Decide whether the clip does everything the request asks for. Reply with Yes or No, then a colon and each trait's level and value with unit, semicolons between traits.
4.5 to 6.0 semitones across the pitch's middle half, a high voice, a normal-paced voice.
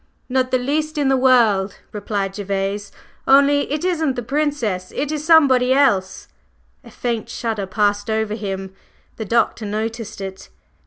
Yes: average, 5.2 semitones; high, 230 Hz; average, 150 wpm